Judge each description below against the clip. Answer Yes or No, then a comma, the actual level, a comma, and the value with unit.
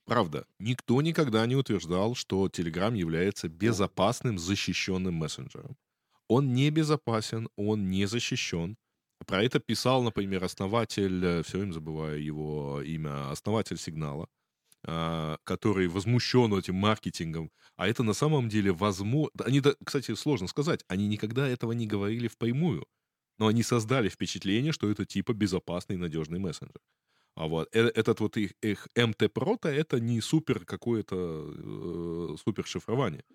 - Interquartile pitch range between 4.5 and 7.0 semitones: Yes, average, 4.8 semitones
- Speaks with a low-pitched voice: Yes, low, 105 Hz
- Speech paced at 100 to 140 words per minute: Yes, average, 130 wpm